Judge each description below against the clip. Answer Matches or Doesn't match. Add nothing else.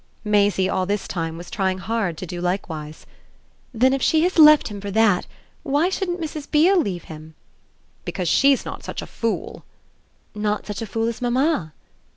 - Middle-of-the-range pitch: Doesn't match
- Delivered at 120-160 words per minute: Doesn't match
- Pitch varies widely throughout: Matches